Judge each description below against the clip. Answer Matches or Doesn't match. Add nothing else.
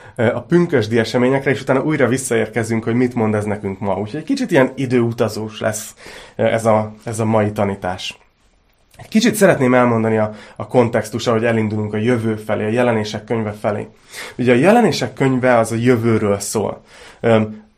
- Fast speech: Matches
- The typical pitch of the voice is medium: Doesn't match